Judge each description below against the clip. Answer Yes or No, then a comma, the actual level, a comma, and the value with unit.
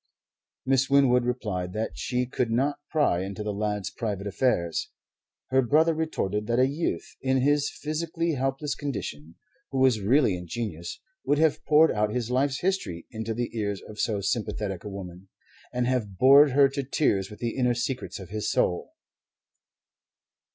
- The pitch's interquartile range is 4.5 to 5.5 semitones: Yes, average, 5.1 semitones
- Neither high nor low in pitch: No, low, 120 Hz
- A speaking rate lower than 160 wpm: No, average, 165 wpm